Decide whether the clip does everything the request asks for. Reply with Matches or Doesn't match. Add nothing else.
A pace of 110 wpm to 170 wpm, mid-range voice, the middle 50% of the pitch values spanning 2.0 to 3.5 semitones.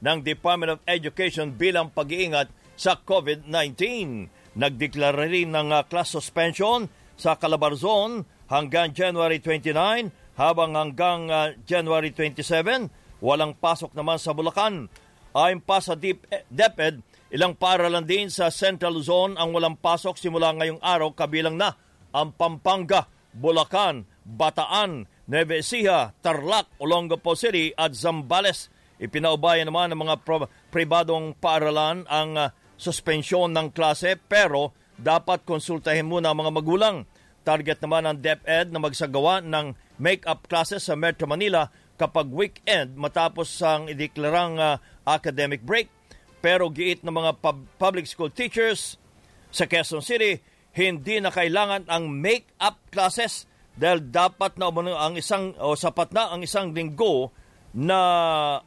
Matches